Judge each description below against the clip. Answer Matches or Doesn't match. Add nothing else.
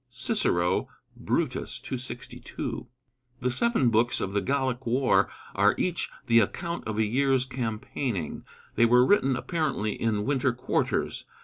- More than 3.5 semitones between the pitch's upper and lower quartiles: Doesn't match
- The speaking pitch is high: Doesn't match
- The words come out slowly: Matches